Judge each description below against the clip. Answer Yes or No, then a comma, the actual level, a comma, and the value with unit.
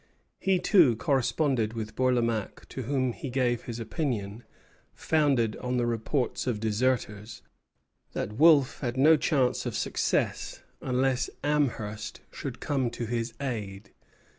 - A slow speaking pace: Yes, slow, 130 wpm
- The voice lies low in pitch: Yes, low, 125 Hz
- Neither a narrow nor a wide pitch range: Yes, average, 3.3 semitones